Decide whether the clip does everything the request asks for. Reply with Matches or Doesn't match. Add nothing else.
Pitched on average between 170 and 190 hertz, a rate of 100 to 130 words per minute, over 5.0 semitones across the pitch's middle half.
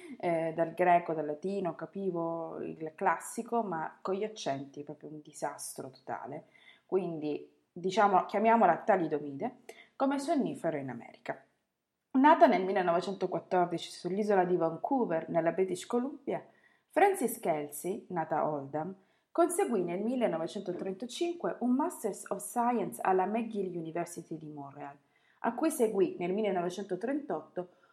Matches